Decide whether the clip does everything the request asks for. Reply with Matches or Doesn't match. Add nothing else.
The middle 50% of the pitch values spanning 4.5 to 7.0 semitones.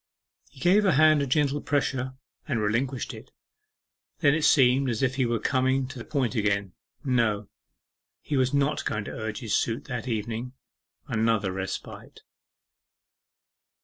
Doesn't match